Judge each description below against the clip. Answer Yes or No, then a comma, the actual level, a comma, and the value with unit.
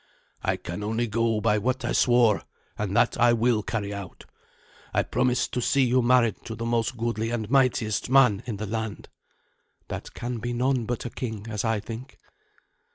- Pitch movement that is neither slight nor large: No, narrow, 2.3 semitones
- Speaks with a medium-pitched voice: No, low, 115 Hz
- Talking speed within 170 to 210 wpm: Yes, average, 185 wpm